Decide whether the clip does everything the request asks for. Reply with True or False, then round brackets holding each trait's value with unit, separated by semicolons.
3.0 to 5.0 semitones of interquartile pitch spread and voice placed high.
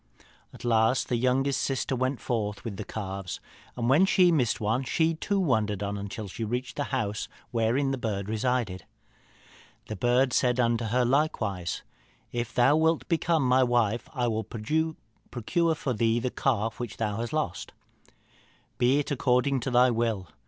False (3.6 semitones; 120 Hz)